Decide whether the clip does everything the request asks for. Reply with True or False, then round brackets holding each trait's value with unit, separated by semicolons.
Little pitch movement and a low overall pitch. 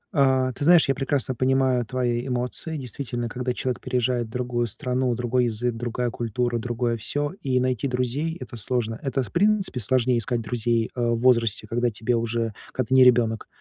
True (1.8 semitones; 125 Hz)